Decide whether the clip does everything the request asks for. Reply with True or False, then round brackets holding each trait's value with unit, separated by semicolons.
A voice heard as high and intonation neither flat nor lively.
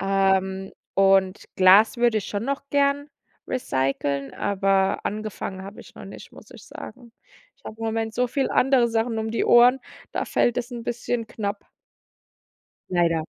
True (215 Hz; 3.8 semitones)